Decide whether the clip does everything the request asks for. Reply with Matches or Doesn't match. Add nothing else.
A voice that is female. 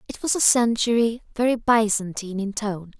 Matches